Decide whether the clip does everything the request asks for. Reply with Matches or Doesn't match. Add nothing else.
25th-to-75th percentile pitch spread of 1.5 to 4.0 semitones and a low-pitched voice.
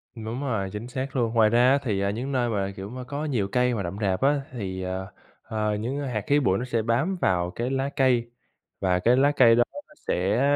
Doesn't match